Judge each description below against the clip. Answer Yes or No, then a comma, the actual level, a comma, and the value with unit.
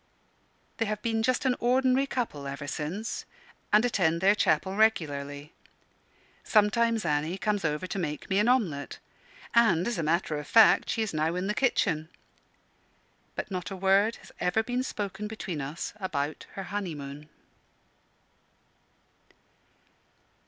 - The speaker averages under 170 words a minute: Yes, average, 140 wpm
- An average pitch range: No, wide, 6.2 semitones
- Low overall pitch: No, high, 190 Hz